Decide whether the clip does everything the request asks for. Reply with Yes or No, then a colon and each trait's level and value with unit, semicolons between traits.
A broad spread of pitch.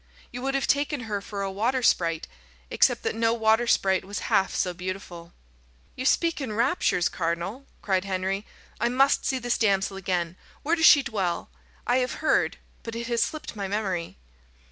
No: average, 5.0 semitones